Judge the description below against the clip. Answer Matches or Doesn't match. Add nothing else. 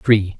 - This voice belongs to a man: Matches